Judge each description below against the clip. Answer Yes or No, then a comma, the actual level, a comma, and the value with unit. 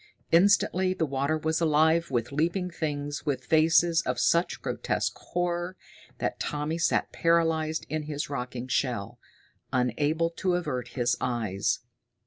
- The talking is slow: Yes, slow, 130 wpm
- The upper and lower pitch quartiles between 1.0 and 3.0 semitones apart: No, average, 4.5 semitones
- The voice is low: No, medium, 155 Hz